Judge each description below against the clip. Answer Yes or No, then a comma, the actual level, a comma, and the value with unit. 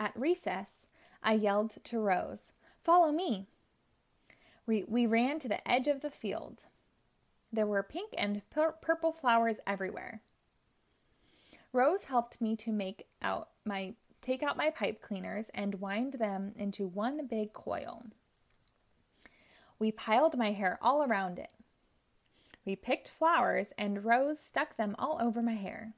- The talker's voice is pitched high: Yes, high, 225 Hz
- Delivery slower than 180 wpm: Yes, average, 145 wpm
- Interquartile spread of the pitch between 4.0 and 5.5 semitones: Yes, average, 5.2 semitones